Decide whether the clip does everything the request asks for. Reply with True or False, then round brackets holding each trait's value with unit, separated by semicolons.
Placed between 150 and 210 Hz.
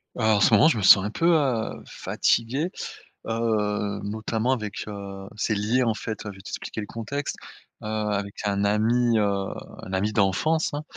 False (110 Hz)